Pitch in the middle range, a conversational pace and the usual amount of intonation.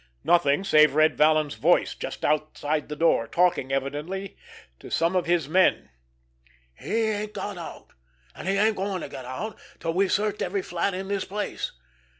Yes: medium, 170 Hz; average, 165 wpm; average, 4.5 semitones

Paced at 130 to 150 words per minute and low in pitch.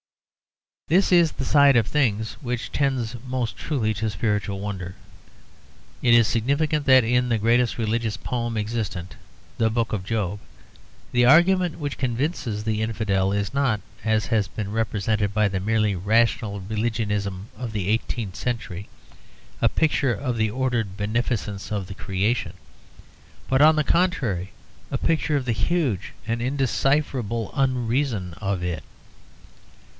Yes: average, 140 wpm; low, 115 Hz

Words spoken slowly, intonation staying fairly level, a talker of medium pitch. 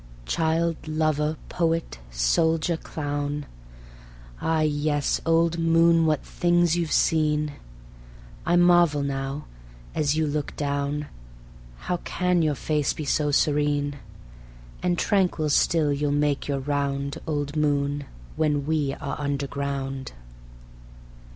Yes: slow, 110 wpm; narrow, 2.2 semitones; medium, 150 Hz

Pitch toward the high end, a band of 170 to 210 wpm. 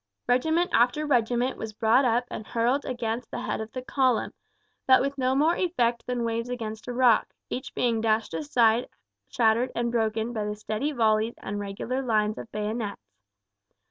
Yes: high, 235 Hz; average, 175 wpm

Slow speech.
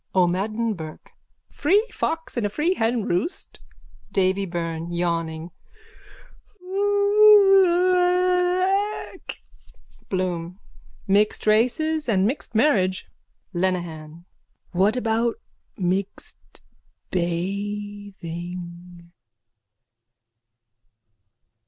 Yes: slow, 65 wpm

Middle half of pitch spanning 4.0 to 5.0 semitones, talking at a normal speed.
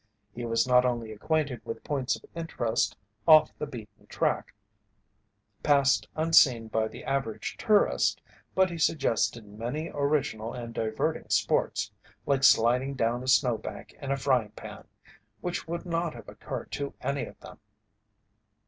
Yes: average, 4.6 semitones; average, 145 wpm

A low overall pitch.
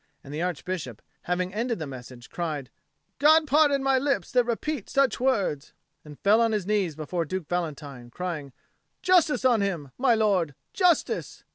No: medium, 185 Hz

